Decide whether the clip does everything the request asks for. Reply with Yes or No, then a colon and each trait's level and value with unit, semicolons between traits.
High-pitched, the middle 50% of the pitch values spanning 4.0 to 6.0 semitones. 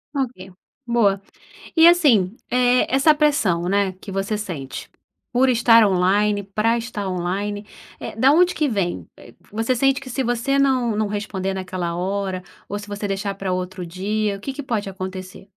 Yes: high, 205 Hz; average, 4.5 semitones